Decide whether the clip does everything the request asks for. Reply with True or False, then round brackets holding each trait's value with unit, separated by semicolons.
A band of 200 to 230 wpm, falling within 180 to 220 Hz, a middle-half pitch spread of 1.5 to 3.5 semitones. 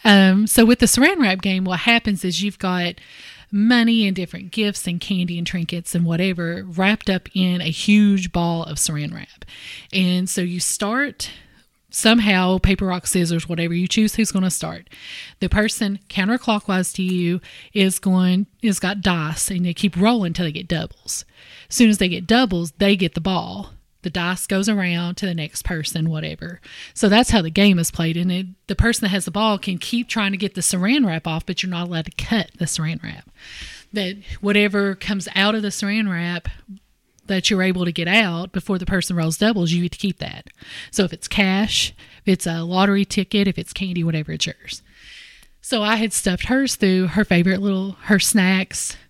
True (205 wpm; 190 Hz; 2.8 semitones)